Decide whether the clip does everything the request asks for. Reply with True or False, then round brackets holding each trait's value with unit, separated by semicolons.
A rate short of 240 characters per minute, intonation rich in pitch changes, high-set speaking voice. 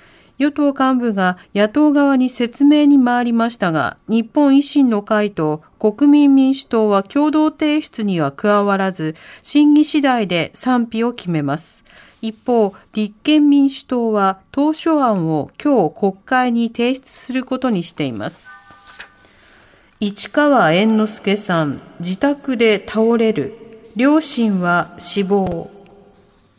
True (225 characters per minute; 6.1 semitones; 225 Hz)